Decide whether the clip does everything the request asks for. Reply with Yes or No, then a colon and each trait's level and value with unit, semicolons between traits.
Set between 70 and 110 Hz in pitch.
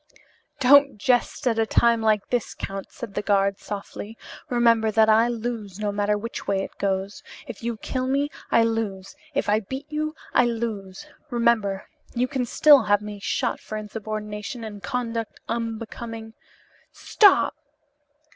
No: high, 225 Hz